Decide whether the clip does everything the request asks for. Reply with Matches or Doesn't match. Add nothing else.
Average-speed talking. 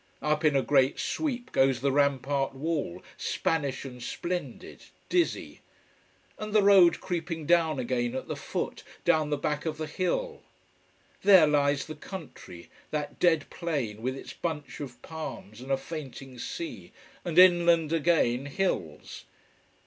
Matches